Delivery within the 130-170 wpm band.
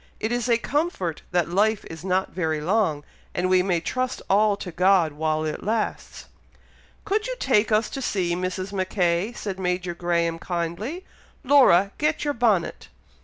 Yes: average, 165 wpm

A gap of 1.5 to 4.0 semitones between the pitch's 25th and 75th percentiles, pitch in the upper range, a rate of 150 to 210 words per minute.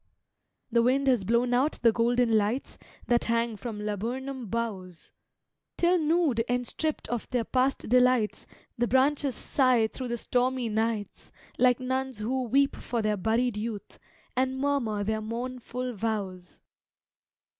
No: average, 2.8 semitones; high, 240 Hz; average, 140 wpm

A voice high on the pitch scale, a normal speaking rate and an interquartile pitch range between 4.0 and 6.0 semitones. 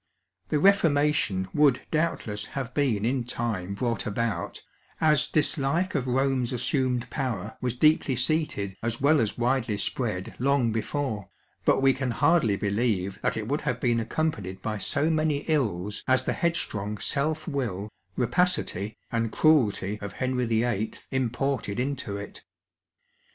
No: low, 125 Hz; average, 145 wpm; average, 4.9 semitones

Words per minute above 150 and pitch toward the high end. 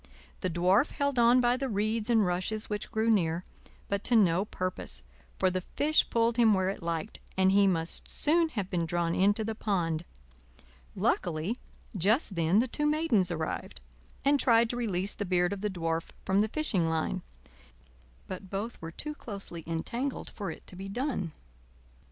Yes: average, 175 wpm; high, 200 Hz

